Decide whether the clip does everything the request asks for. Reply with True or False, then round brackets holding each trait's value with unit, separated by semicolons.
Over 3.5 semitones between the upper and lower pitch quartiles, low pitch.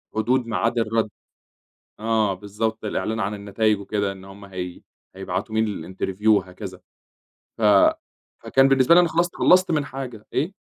True (3.9 semitones; 110 Hz)